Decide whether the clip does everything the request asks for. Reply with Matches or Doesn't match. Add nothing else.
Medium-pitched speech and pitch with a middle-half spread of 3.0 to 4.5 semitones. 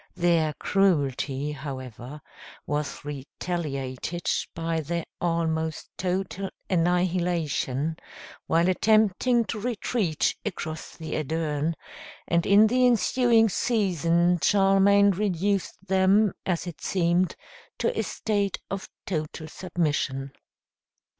Matches